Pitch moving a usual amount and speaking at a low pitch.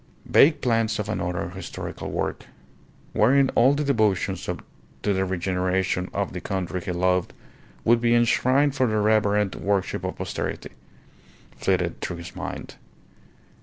Yes: average, 4.3 semitones; low, 105 Hz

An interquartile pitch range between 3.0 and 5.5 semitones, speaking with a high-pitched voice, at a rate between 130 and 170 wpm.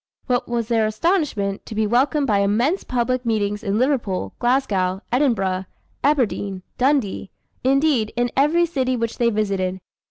Yes: average, 4.8 semitones; high, 235 Hz; average, 140 wpm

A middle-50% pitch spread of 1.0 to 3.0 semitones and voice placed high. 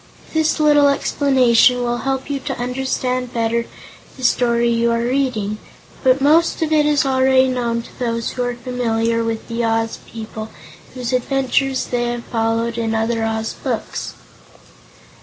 Yes: narrow, 2.4 semitones; high, 245 Hz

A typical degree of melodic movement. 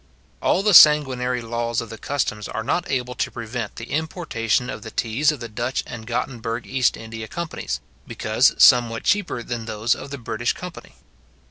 Yes: average, 3.2 semitones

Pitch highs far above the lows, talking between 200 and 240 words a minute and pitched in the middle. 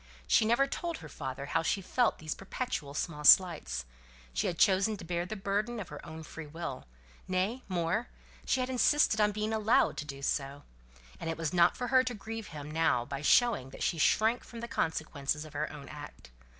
Yes: wide, 6.7 semitones; fast, 205 wpm; medium, 175 Hz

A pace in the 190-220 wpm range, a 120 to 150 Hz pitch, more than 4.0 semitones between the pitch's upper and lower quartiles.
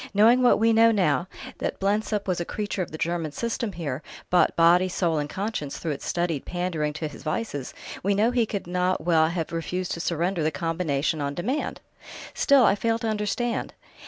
No: average, 195 wpm; medium, 180 Hz; average, 4.7 semitones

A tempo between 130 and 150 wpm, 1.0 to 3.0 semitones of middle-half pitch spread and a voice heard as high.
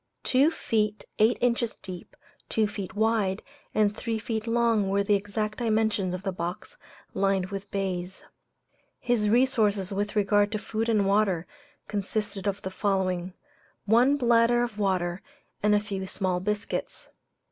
Yes: average, 145 wpm; narrow, 2.5 semitones; high, 205 Hz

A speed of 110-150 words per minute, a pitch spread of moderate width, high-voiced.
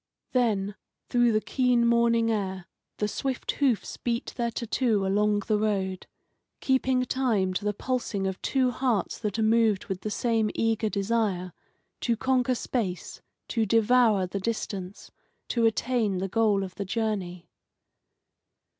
Yes: average, 145 wpm; average, 3.2 semitones; high, 220 Hz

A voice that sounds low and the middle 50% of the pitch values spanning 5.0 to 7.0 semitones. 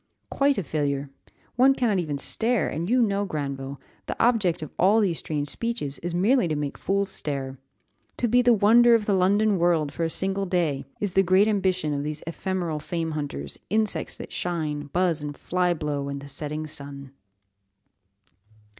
No: medium, 175 Hz; wide, 5.6 semitones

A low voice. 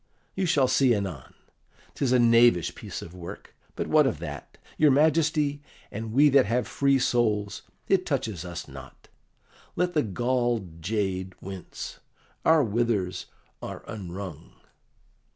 Yes: low, 115 Hz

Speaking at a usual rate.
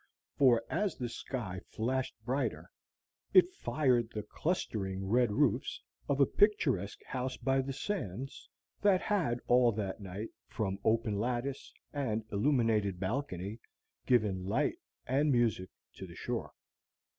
No: slow, 130 wpm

